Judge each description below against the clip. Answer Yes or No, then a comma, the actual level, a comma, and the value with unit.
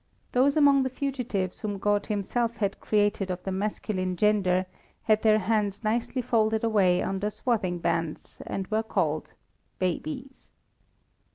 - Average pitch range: Yes, average, 3.5 semitones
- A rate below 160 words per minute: Yes, average, 140 wpm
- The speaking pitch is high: Yes, high, 210 Hz